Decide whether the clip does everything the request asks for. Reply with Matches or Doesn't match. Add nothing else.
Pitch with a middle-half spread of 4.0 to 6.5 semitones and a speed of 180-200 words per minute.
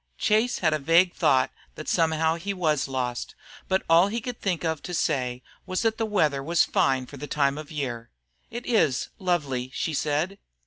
Matches